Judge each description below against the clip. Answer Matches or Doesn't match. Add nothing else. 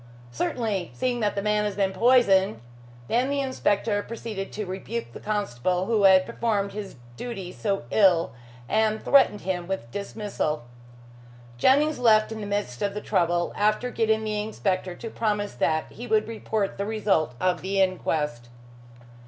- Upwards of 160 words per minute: Doesn't match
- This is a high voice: Matches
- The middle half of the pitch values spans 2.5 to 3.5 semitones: Matches